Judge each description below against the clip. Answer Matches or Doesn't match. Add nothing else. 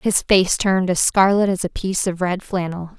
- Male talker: Doesn't match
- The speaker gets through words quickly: Matches